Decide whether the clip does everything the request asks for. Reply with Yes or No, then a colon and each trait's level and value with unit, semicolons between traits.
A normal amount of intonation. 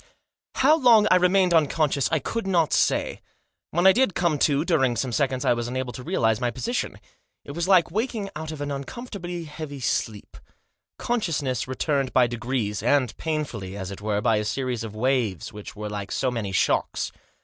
No: wide, 6.6 semitones